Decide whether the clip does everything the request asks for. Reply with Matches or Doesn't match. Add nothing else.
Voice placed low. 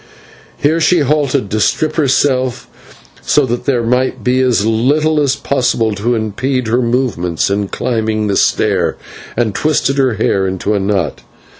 Matches